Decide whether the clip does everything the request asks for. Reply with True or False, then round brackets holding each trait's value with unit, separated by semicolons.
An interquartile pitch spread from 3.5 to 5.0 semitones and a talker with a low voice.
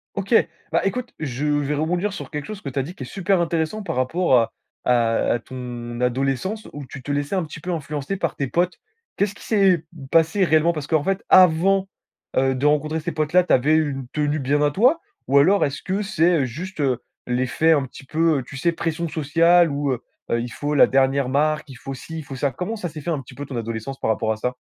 False (4.4 semitones; 150 Hz)